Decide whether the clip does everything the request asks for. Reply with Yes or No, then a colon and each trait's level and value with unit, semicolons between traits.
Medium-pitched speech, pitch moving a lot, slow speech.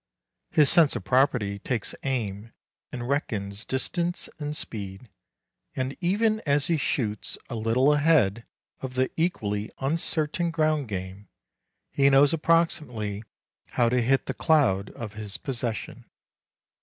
No: low, 130 Hz; wide, 6.0 semitones; slow, 130 wpm